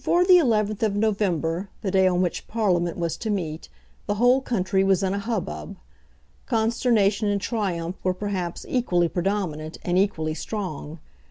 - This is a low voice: No, high, 195 Hz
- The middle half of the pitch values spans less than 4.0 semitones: Yes, average, 3.6 semitones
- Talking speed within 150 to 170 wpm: Yes, average, 160 wpm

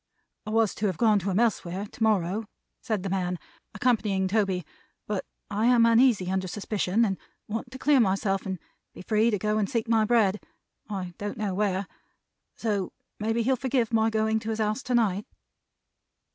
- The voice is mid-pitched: No, high, 215 Hz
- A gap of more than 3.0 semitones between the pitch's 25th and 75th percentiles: No, average, 2.7 semitones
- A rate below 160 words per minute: No, average, 185 wpm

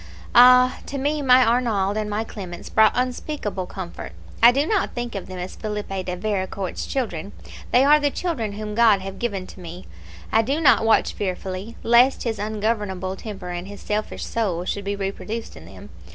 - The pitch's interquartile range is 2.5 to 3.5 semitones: No, average, 4.0 semitones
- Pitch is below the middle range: No, high, 215 Hz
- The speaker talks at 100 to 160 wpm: No, average, 185 wpm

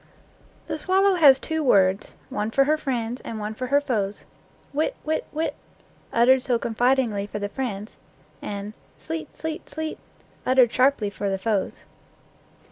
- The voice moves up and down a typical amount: No, wide, 6.0 semitones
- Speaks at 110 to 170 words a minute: Yes, average, 150 wpm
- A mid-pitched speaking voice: No, very high, 250 Hz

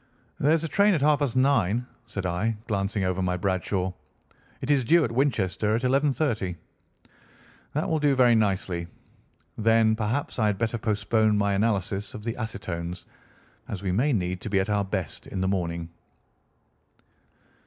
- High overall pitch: No, low, 105 Hz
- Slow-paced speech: No, average, 165 wpm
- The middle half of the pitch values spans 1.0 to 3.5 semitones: No, average, 4.6 semitones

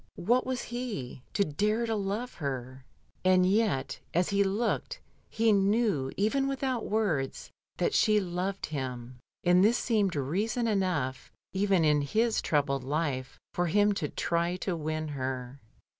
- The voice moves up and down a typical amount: No, wide, 7.0 semitones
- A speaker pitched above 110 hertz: Yes, medium, 185 Hz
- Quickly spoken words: No, average, 145 wpm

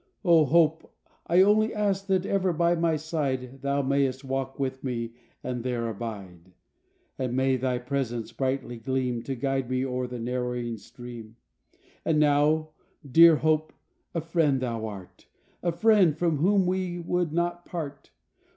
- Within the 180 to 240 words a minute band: No, average, 150 wpm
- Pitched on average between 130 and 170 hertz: Yes, low, 135 Hz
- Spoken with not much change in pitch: No, average, 5.2 semitones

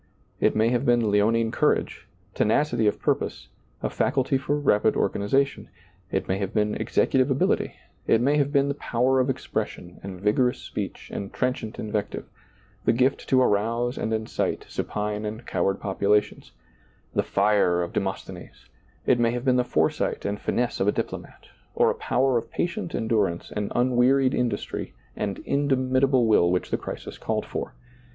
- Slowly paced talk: No, average, 170 wpm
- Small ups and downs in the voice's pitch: No, average, 3.9 semitones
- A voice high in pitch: No, low, 115 Hz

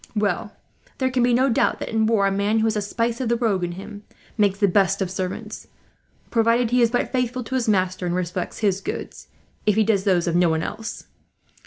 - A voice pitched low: No, high, 210 Hz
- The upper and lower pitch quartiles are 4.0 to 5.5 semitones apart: No, average, 3.5 semitones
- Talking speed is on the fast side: Yes, fast, 230 wpm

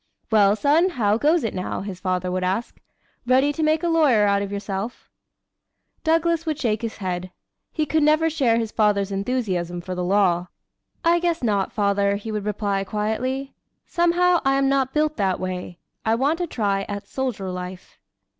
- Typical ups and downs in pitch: No, wide, 6.9 semitones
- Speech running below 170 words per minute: No, average, 180 wpm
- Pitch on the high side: Yes, high, 220 Hz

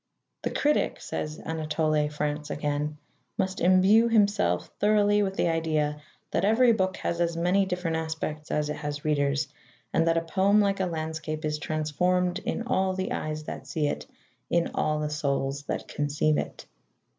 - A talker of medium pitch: Yes, medium, 160 Hz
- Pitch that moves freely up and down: No, average, 3.9 semitones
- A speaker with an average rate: Yes, average, 170 wpm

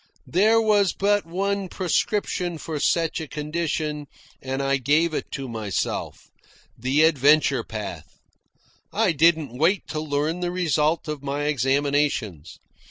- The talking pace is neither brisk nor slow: No, slow, 130 wpm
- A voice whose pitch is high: No, medium, 155 Hz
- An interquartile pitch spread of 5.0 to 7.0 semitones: No, average, 3.9 semitones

